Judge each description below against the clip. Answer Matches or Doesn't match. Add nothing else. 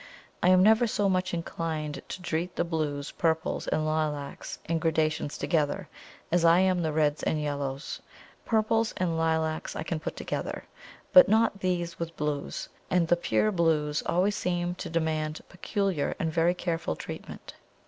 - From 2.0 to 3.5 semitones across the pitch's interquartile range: Matches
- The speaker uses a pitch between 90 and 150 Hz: Doesn't match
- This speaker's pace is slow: Doesn't match